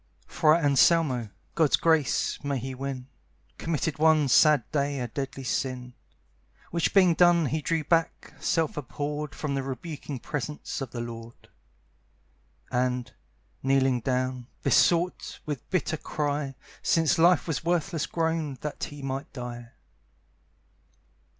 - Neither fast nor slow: No, slow, 125 wpm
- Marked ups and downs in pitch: No, average, 3.7 semitones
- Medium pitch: Yes, medium, 145 Hz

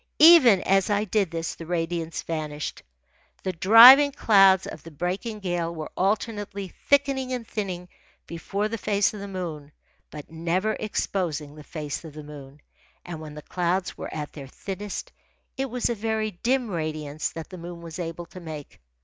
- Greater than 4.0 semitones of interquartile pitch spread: Yes, average, 4.7 semitones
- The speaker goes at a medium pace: Yes, average, 175 wpm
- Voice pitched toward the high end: No, medium, 180 Hz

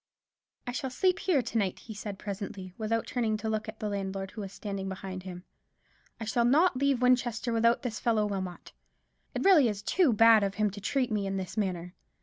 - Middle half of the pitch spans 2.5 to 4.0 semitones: Yes, average, 3.5 semitones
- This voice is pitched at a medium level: No, high, 215 Hz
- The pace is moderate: No, fast, 210 wpm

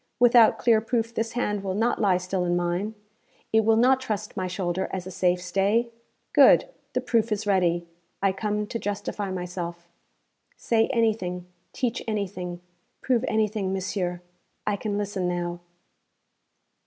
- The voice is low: No, high, 200 Hz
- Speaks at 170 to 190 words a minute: No, average, 150 wpm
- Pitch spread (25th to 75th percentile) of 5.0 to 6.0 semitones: No, average, 3.7 semitones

